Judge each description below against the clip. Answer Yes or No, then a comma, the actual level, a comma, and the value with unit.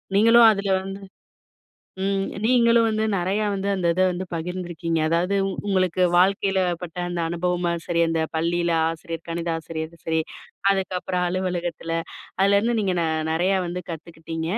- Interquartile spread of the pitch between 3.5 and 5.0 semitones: No, average, 2.7 semitones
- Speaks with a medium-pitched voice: Yes, medium, 180 Hz